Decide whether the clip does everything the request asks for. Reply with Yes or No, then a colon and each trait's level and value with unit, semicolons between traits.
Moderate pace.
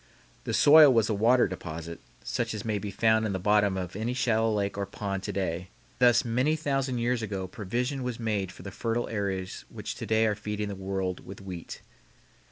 No: fast, 210 wpm